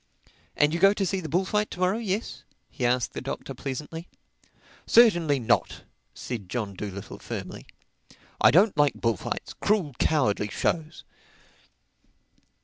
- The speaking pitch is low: No, medium, 160 Hz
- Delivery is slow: Yes, slow, 130 wpm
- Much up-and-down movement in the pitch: Yes, wide, 7.4 semitones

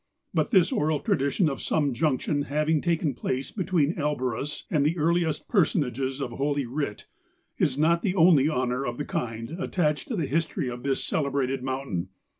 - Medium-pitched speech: Yes, medium, 145 Hz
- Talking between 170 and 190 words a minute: Yes, average, 175 wpm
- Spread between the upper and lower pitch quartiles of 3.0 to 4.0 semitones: Yes, average, 3.4 semitones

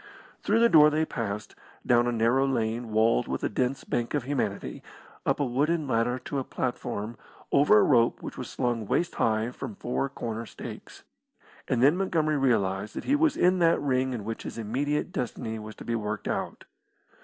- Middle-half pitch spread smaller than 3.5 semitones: No, average, 4.3 semitones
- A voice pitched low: Yes, low, 125 Hz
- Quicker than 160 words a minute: Yes, average, 190 wpm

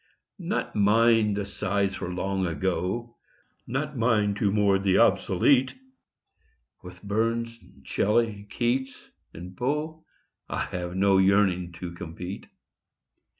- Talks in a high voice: No, low, 100 Hz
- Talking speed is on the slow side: Yes, slow, 115 wpm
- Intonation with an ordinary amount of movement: Yes, average, 4.0 semitones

